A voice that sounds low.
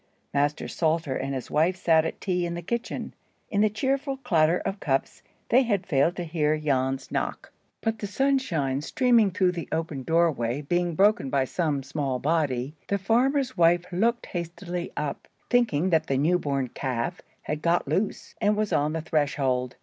No: medium, 165 Hz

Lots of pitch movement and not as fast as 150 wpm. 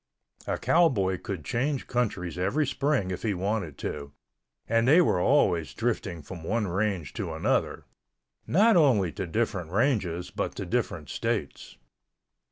Yes: wide, 5.8 semitones; average, 140 wpm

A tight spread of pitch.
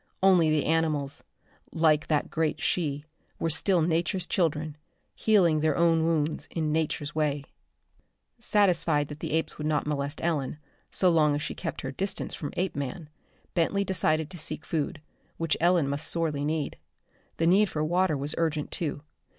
Yes: narrow, 2.3 semitones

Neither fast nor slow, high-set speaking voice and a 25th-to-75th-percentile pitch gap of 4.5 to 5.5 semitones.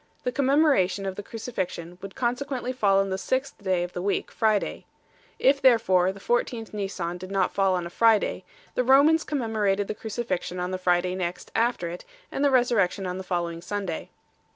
Yes: average, 190 wpm; high, 200 Hz; average, 4.8 semitones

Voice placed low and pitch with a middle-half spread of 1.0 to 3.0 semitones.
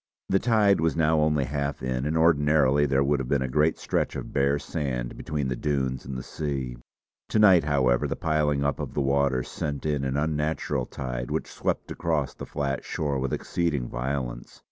Yes: very low, 70 Hz; narrow, 2.6 semitones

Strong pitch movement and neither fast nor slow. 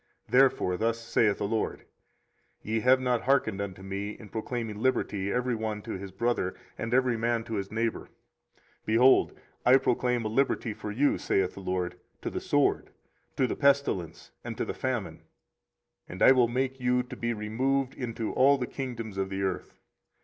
No: average, 3.5 semitones; average, 180 wpm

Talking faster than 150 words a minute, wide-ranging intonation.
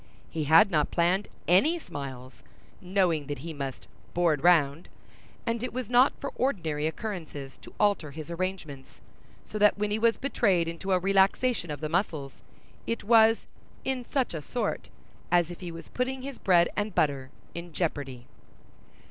Yes: average, 165 wpm; wide, 5.8 semitones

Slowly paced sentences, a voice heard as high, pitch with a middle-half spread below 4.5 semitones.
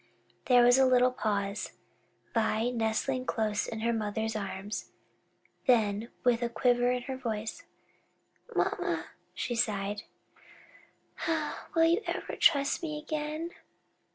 Yes: slow, 125 wpm; high, 240 Hz; average, 3.2 semitones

